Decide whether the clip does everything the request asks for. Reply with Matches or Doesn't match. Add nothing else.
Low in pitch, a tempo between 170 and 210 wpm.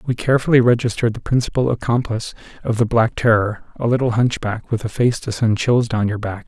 Matches